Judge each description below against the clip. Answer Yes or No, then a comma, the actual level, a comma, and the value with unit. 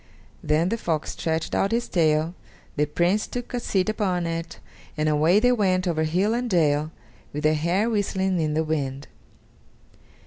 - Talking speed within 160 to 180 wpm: Yes, average, 170 wpm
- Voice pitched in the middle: Yes, medium, 170 Hz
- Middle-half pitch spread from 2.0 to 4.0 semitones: No, average, 4.4 semitones